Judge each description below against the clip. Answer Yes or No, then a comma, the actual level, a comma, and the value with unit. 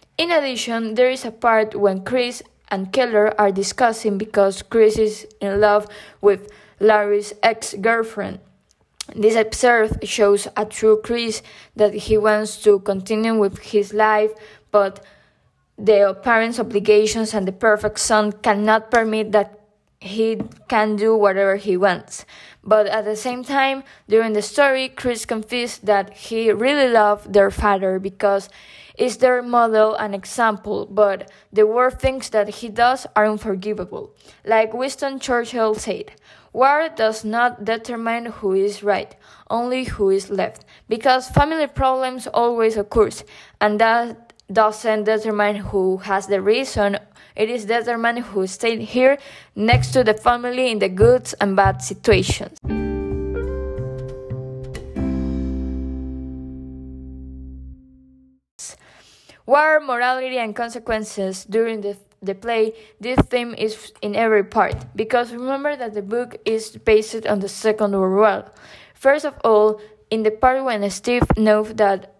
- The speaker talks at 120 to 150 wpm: Yes, slow, 135 wpm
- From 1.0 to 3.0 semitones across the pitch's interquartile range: Yes, narrow, 2.6 semitones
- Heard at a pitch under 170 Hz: No, high, 215 Hz